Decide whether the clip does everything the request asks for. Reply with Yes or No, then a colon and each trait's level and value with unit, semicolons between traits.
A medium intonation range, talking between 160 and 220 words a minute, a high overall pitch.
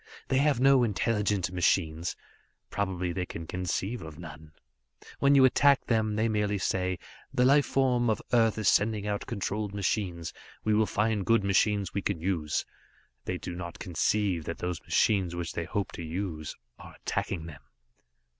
No: average, 4.1 semitones; average, 165 wpm; low, 100 Hz